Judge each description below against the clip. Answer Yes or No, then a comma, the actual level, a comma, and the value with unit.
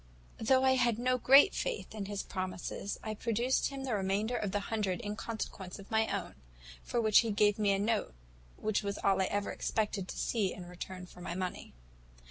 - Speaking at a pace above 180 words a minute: Yes, fast, 205 wpm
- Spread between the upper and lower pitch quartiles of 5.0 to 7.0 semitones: No, average, 3.1 semitones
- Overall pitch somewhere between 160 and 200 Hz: No, high, 210 Hz